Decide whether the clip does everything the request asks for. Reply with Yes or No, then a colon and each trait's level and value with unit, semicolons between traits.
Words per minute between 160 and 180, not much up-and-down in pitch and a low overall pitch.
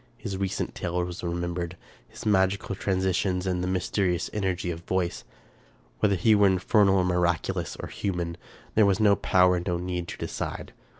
Yes: average, 165 wpm; narrow, 1.8 semitones; very low, 90 Hz